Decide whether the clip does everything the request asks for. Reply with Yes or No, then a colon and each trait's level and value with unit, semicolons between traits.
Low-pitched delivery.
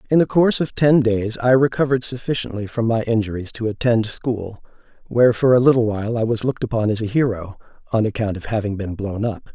Yes: low, 115 Hz